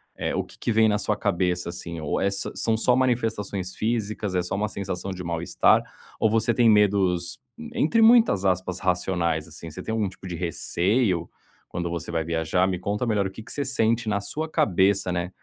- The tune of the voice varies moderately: Yes, average, 4.0 semitones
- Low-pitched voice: Yes, very low, 95 Hz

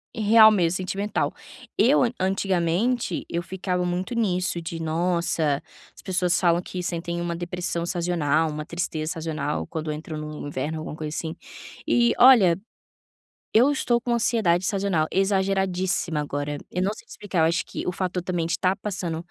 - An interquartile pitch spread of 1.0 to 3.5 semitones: Yes, average, 2.9 semitones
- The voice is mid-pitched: Yes, medium, 175 Hz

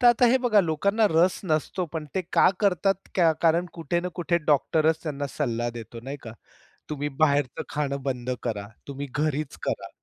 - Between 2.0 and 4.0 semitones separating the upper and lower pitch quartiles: No, average, 4.4 semitones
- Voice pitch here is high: No, medium, 155 Hz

